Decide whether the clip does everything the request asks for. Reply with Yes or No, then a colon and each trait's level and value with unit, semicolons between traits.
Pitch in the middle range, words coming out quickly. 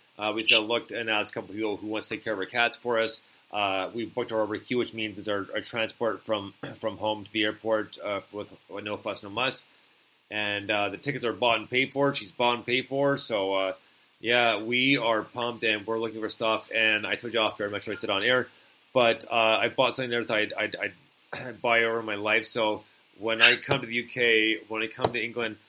No: low, 110 Hz; fast, 255 wpm